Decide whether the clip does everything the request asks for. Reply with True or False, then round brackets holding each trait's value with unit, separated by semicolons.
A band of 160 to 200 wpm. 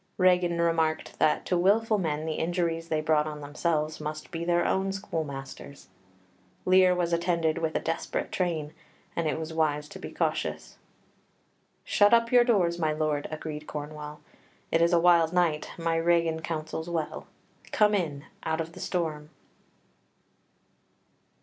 False (150 wpm)